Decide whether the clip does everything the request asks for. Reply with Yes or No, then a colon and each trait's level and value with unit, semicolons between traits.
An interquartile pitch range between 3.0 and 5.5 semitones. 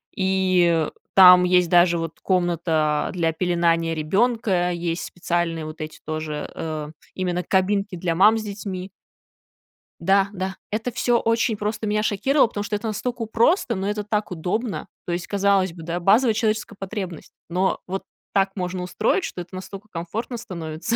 Yes: average, 3.5 semitones